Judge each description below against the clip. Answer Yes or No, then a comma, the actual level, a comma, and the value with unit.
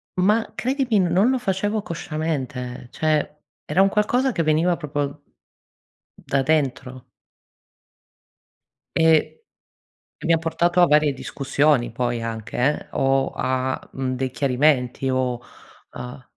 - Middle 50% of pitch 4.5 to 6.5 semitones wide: Yes, average, 5.1 semitones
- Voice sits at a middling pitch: Yes, medium, 150 Hz